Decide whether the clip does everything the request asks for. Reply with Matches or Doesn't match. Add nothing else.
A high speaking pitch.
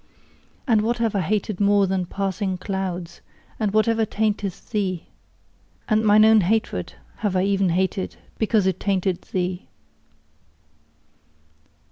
Matches